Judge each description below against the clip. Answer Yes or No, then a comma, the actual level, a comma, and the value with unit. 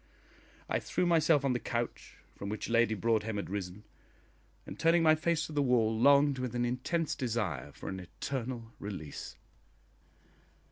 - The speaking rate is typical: Yes, average, 155 wpm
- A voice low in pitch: Yes, low, 120 Hz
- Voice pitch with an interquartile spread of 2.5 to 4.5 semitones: No, average, 5.1 semitones